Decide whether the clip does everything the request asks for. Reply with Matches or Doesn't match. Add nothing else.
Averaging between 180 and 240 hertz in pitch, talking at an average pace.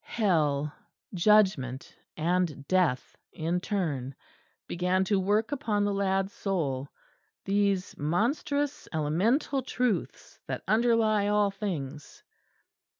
Doesn't match